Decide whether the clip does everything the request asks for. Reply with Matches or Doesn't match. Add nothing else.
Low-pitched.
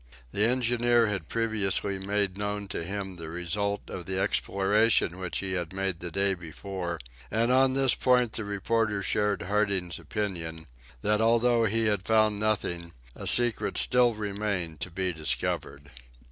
Matches